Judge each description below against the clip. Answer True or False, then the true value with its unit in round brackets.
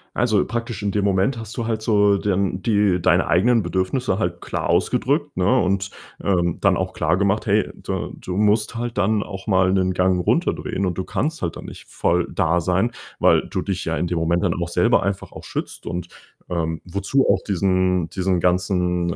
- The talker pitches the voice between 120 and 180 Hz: False (95 Hz)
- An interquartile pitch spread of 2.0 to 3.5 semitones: True (2.7 semitones)